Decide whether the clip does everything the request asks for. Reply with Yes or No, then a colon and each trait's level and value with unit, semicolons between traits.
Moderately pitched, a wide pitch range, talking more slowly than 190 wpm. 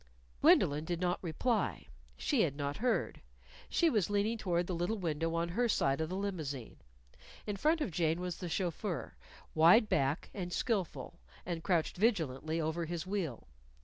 No: medium, 175 Hz; average, 4.2 semitones; average, 165 wpm